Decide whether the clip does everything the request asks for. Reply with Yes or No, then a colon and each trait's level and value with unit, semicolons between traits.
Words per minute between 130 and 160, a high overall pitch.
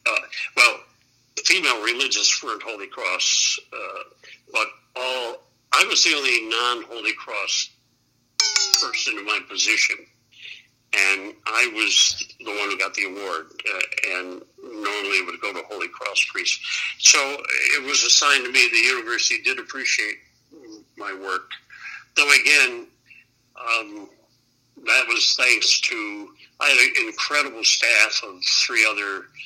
Yes: slow, 135 wpm; very high, 325 Hz